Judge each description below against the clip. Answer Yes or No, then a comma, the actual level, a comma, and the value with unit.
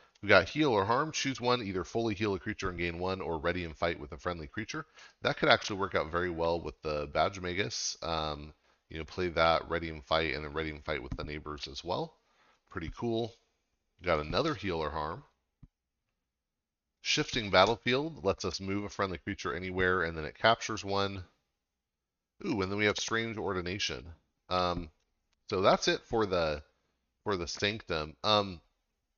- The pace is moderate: Yes, average, 185 wpm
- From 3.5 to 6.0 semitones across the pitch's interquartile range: Yes, average, 4.2 semitones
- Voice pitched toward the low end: Yes, very low, 90 Hz